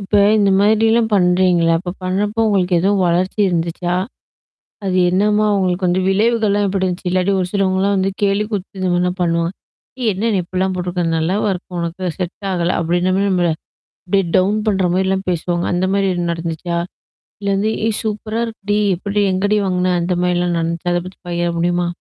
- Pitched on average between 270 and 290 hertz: No, medium, 185 Hz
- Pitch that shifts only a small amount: Yes, narrow, 2.2 semitones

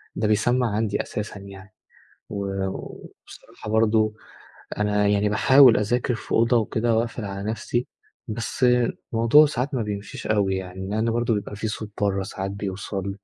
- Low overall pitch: Yes, low, 105 Hz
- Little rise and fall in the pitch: Yes, narrow, 2.3 semitones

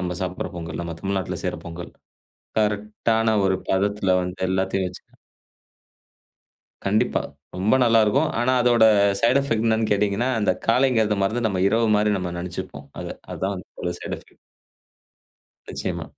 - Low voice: Yes, low, 100 Hz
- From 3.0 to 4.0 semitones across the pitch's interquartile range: Yes, average, 3.3 semitones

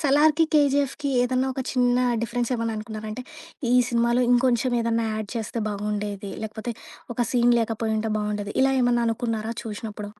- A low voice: No, high, 230 Hz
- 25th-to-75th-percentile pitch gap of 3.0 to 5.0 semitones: No, narrow, 2.5 semitones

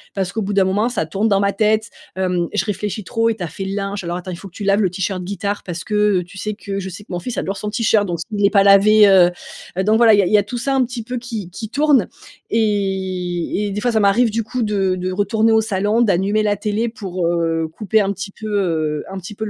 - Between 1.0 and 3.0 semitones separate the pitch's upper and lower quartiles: Yes, narrow, 2.5 semitones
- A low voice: No, high, 200 Hz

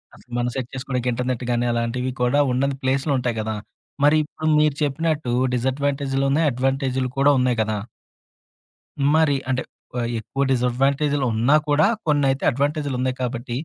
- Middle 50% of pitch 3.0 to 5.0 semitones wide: No, narrow, 2.4 semitones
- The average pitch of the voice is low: Yes, low, 130 Hz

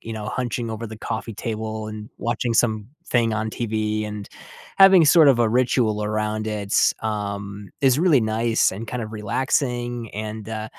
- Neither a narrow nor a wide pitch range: No, narrow, 2.1 semitones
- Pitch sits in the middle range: No, low, 110 Hz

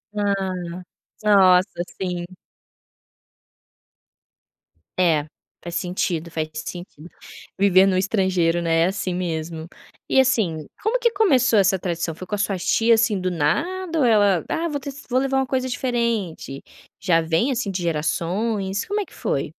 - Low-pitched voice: No, high, 190 Hz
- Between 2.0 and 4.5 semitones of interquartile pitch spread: No, wide, 5.4 semitones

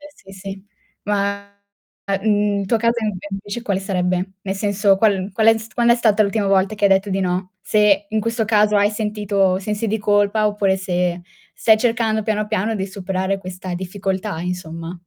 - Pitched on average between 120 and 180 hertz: No, high, 200 Hz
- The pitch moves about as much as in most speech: No, narrow, 1.9 semitones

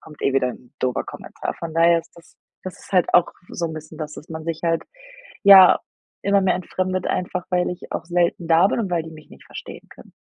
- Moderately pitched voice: Yes, medium, 170 Hz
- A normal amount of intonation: No, narrow, 2.3 semitones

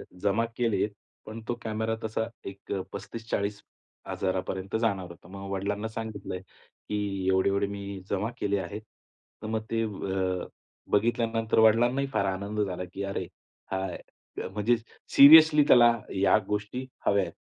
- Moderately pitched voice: No, low, 105 Hz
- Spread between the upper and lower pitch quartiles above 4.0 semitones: No, narrow, 2.6 semitones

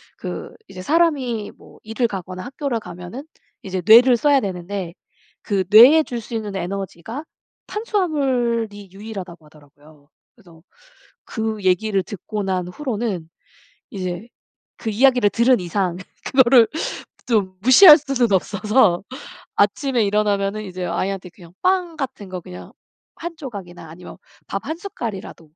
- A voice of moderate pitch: No, high, 210 Hz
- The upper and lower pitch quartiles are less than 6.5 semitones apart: Yes, wide, 5.4 semitones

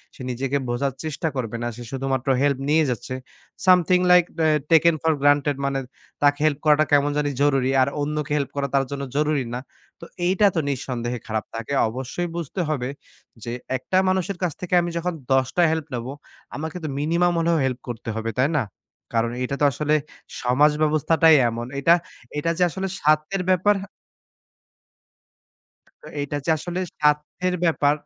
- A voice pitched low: No, medium, 145 Hz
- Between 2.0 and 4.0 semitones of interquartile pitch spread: Yes, average, 3.7 semitones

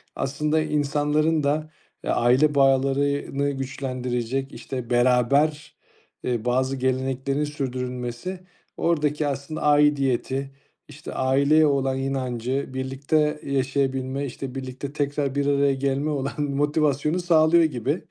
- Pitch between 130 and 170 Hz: Yes, medium, 140 Hz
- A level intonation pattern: Yes, narrow, 2.0 semitones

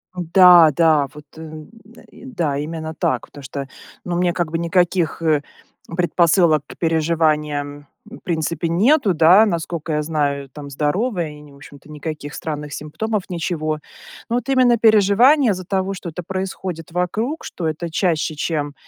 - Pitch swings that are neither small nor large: Yes, average, 3.5 semitones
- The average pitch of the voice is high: No, medium, 165 Hz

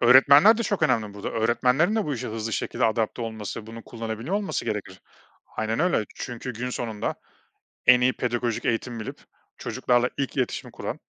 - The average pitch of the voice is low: Yes, low, 120 Hz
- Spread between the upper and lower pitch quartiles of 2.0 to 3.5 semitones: Yes, average, 2.8 semitones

